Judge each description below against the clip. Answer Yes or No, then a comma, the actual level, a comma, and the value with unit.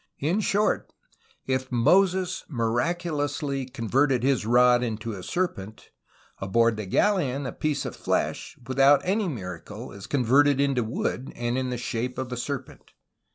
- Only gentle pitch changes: No, average, 3.8 semitones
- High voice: No, low, 130 Hz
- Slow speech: No, average, 150 wpm